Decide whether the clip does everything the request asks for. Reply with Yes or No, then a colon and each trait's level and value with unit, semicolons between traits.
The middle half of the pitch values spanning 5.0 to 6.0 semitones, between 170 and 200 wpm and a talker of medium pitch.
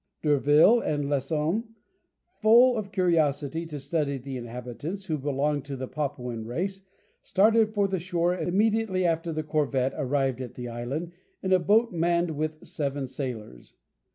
No: average, 5.3 semitones; average, 150 wpm; medium, 155 Hz